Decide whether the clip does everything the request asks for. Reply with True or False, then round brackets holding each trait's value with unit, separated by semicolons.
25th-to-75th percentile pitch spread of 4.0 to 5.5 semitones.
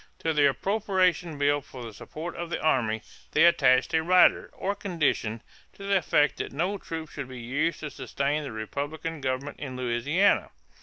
True (4.7 semitones)